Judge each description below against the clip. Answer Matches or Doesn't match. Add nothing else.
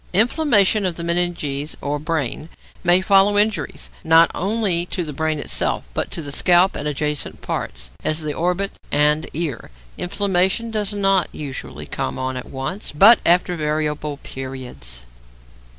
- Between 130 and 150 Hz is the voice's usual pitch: Doesn't match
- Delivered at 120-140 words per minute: Doesn't match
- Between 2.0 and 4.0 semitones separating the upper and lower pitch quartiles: Doesn't match